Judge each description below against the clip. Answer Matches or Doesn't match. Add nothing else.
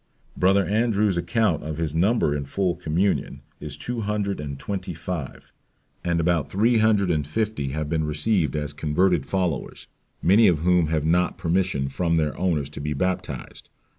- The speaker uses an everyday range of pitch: Matches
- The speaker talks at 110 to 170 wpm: Matches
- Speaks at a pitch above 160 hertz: Doesn't match